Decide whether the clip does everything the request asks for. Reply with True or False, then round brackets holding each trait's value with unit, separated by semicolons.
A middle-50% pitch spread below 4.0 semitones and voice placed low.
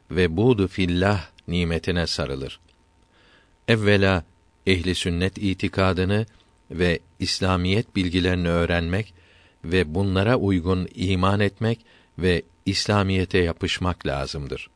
True (2.4 semitones; 90 Hz)